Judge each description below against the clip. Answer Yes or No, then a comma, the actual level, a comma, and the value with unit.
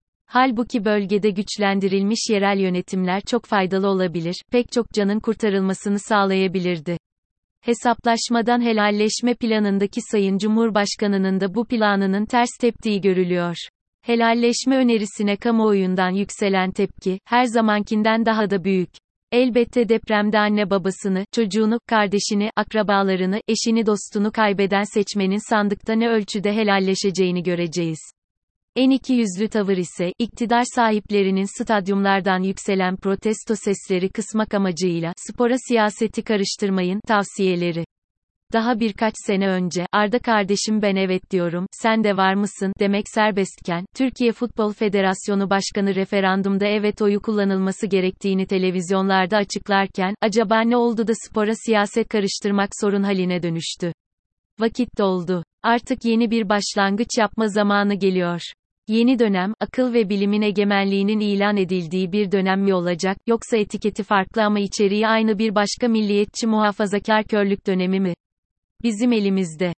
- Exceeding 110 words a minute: Yes, average, 120 wpm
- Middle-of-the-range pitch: No, high, 205 Hz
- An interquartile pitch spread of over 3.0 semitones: No, narrow, 2.5 semitones